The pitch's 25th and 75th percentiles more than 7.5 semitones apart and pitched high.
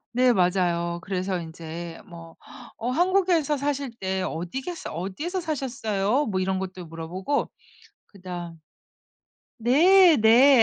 Yes: wide, 8.1 semitones; high, 195 Hz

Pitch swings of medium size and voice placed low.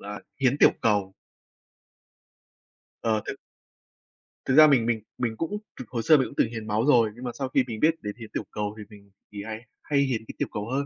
Yes: average, 3.9 semitones; low, 115 Hz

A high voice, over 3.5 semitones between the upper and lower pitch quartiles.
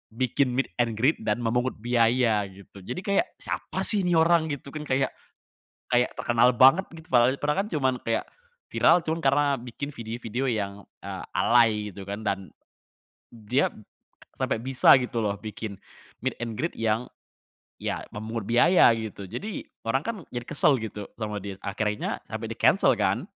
No: low, 120 Hz; average, 4.0 semitones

